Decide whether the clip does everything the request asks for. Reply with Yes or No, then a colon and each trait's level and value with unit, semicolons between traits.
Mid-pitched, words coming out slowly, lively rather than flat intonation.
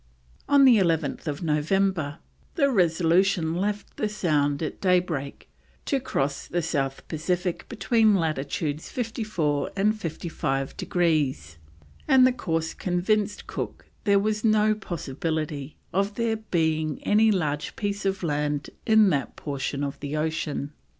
Yes: medium, 170 Hz; slow, 125 wpm; wide, 5.7 semitones